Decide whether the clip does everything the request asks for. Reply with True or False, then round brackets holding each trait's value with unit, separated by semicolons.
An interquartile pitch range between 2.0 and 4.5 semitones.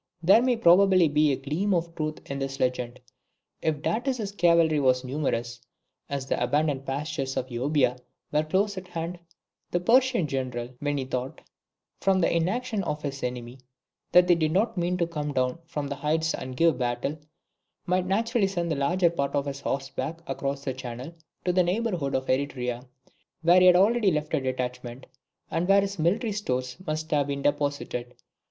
False (5.1 semitones)